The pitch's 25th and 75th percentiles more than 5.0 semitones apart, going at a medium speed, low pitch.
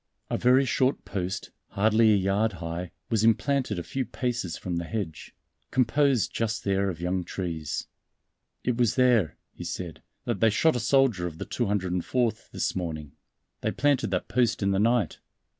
Yes: wide, 5.5 semitones; average, 170 wpm; low, 105 Hz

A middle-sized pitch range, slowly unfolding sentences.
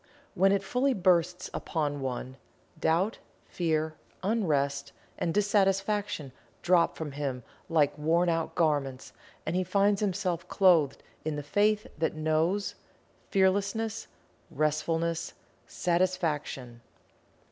Yes: average, 4.4 semitones; slow, 105 wpm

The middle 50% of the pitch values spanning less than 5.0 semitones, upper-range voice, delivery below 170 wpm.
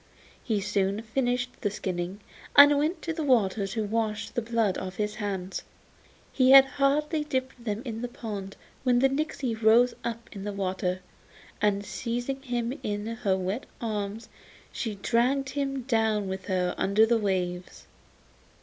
Yes: average, 4.2 semitones; high, 225 Hz; average, 160 wpm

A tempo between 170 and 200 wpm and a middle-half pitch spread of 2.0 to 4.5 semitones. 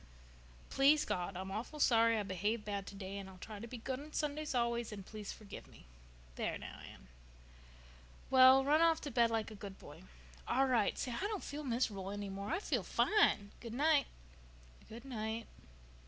No: average, 185 wpm; average, 5.1 semitones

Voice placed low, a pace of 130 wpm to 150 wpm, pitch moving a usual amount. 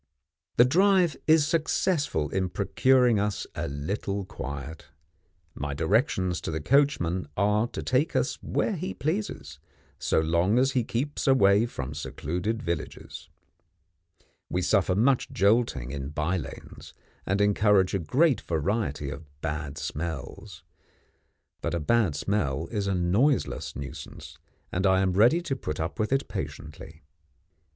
No: low, 100 Hz; average, 140 wpm; wide, 7.7 semitones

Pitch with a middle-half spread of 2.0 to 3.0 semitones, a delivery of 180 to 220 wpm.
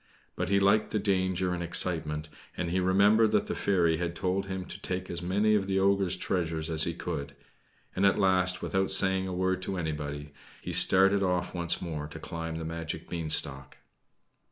Yes: average, 2.7 semitones; average, 190 wpm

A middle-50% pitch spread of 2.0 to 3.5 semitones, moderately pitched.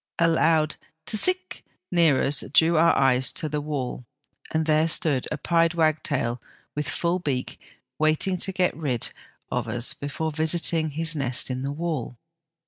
Yes: average, 2.9 semitones; medium, 155 Hz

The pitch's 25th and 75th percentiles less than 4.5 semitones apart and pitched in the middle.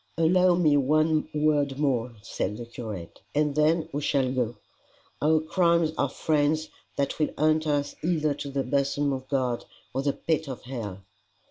Yes: average, 3.0 semitones; medium, 145 Hz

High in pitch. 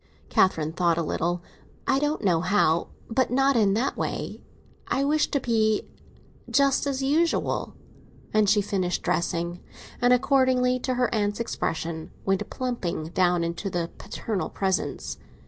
Yes: high, 210 Hz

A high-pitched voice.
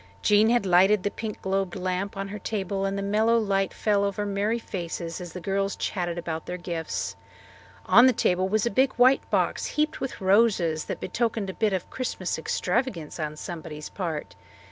Yes: high, 195 Hz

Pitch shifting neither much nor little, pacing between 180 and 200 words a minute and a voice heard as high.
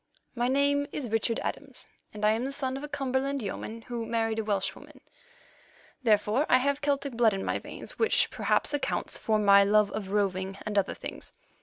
Yes: average, 4.7 semitones; average, 190 wpm; high, 230 Hz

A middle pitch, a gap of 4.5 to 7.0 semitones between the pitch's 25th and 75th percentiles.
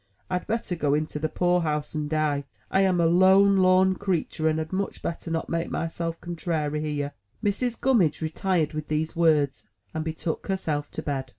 No: medium, 165 Hz; average, 3.3 semitones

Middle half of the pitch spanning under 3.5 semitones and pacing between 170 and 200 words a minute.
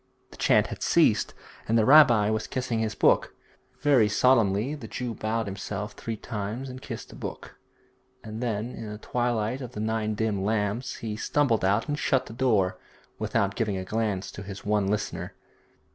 Yes: average, 2.9 semitones; average, 180 wpm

